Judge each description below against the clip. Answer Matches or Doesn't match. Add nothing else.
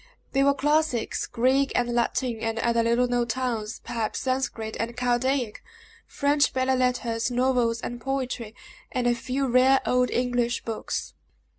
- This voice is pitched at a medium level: Doesn't match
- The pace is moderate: Matches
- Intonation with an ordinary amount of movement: Doesn't match